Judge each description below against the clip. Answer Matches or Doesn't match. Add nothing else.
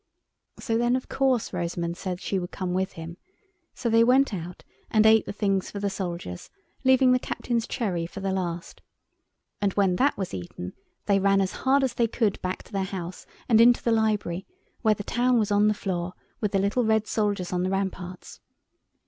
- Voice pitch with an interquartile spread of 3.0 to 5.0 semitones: Matches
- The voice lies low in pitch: Doesn't match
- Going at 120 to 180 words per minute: Doesn't match